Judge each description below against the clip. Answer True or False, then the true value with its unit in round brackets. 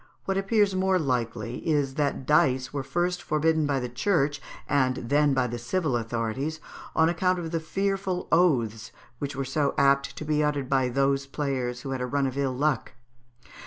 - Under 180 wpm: False (185 wpm)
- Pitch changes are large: False (3.8 semitones)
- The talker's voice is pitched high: False (140 Hz)